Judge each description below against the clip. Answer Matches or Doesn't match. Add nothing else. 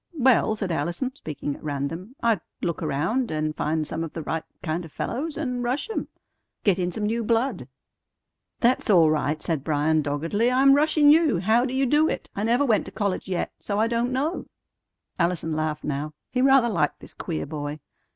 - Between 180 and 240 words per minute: Matches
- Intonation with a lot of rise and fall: Matches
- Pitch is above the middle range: Matches